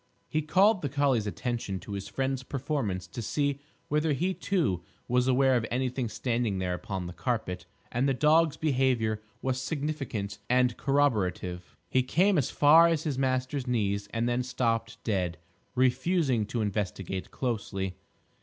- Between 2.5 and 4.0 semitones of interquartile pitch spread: No, average, 5.2 semitones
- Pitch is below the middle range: Yes, low, 125 Hz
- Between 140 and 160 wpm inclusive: Yes, average, 155 wpm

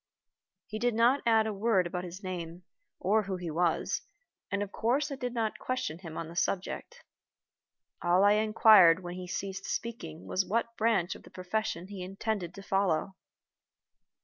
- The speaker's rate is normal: Yes, average, 175 wpm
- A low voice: No, high, 195 Hz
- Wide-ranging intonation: No, average, 3.8 semitones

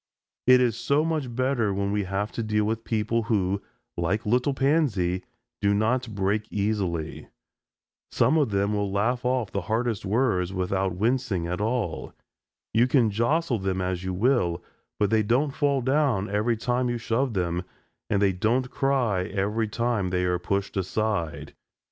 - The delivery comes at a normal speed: Yes, average, 165 wpm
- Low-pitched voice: Yes, low, 110 Hz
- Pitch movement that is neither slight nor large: Yes, average, 4.2 semitones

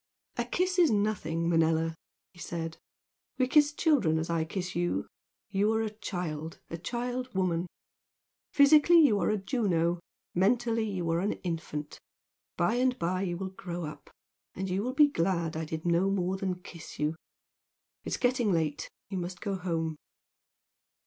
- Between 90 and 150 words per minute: No, average, 160 wpm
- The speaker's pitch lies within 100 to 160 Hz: No, medium, 185 Hz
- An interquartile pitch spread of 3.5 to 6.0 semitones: Yes, average, 5.0 semitones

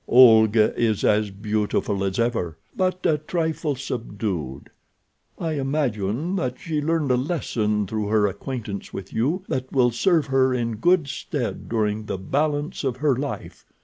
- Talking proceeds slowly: No, average, 150 wpm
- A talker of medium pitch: No, low, 125 Hz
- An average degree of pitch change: No, wide, 5.7 semitones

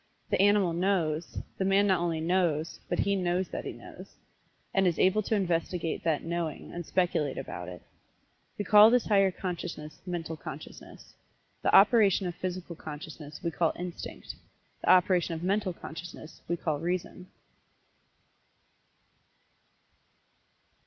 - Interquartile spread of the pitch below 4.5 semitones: Yes, average, 2.7 semitones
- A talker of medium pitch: Yes, medium, 175 Hz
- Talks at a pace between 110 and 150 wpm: Yes, average, 140 wpm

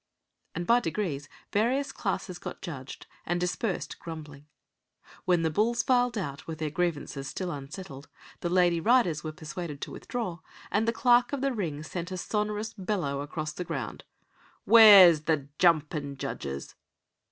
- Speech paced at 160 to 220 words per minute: No, average, 150 wpm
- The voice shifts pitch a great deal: Yes, wide, 5.7 semitones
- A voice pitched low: No, medium, 175 Hz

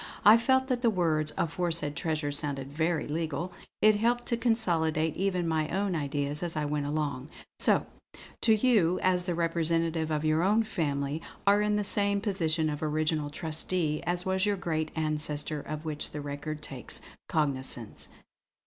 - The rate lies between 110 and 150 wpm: No, average, 165 wpm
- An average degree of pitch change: Yes, average, 3.9 semitones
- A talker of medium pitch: Yes, medium, 160 Hz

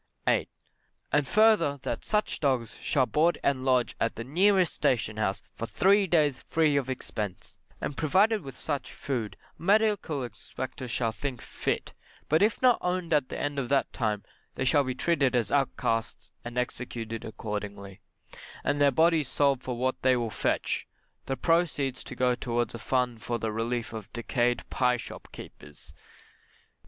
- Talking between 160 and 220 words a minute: Yes, average, 165 wpm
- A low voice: Yes, low, 130 Hz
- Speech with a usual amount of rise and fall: Yes, average, 4.3 semitones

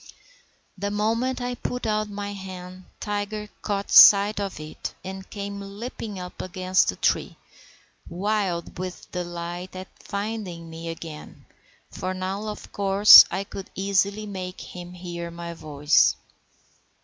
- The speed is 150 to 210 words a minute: No, slow, 135 wpm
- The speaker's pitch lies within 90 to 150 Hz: No, high, 190 Hz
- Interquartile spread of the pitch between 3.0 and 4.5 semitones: No, narrow, 2.5 semitones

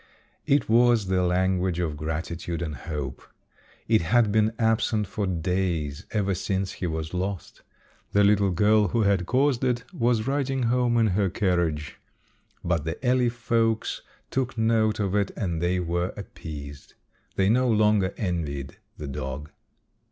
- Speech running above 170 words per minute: No, average, 150 wpm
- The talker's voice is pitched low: Yes, very low, 95 Hz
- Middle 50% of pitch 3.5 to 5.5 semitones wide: Yes, average, 4.8 semitones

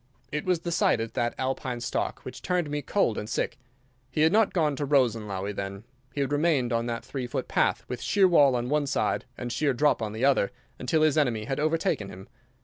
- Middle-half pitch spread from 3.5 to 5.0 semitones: Yes, average, 4.6 semitones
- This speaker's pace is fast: Yes, fast, 225 wpm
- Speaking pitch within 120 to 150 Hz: Yes, low, 135 Hz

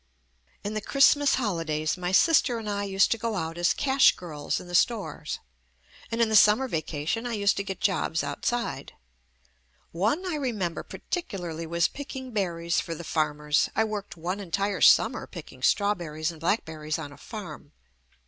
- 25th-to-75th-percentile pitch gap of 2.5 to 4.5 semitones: No, wide, 5.5 semitones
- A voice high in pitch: Yes, high, 195 Hz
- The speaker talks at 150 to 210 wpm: Yes, average, 180 wpm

